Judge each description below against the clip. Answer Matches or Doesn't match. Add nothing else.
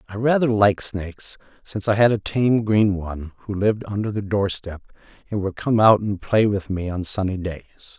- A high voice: Doesn't match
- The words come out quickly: Matches